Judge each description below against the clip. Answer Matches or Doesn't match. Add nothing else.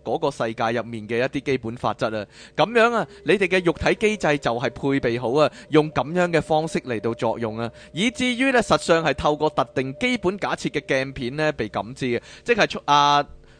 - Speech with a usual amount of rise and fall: Doesn't match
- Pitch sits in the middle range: Matches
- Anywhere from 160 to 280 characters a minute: Doesn't match